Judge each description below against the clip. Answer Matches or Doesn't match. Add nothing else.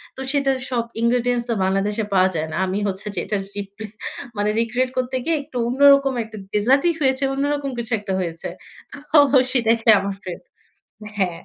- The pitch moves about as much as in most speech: Matches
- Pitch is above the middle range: Matches